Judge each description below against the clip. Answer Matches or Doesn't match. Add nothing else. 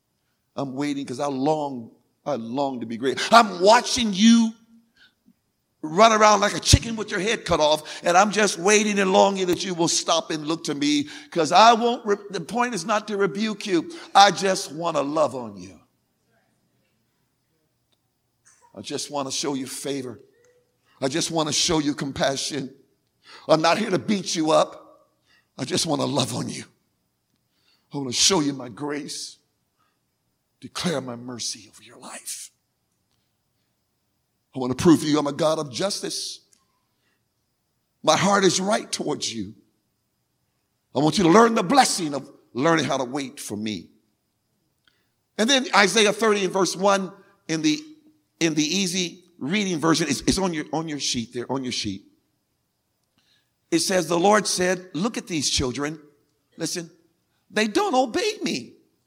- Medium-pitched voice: Matches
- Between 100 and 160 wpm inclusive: Doesn't match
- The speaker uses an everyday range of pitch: Doesn't match